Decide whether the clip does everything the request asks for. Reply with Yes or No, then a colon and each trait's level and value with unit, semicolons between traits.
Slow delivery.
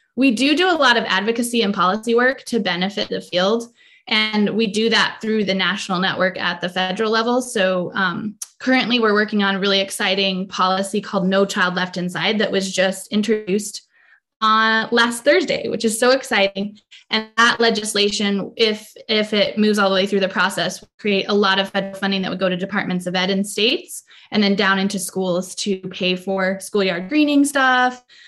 No: average, 195 wpm